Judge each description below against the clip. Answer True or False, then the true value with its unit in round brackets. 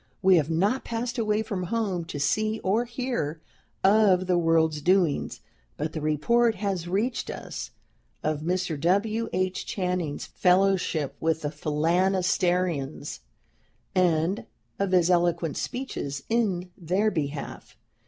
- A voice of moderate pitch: True (180 Hz)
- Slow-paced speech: True (125 wpm)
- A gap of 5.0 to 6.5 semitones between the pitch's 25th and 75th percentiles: False (4.2 semitones)